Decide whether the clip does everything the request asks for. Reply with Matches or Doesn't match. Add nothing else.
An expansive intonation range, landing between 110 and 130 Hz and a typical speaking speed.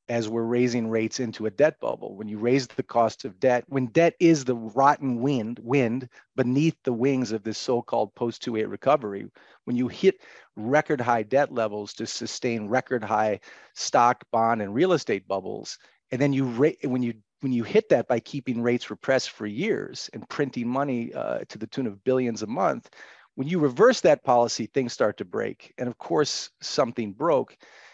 Doesn't match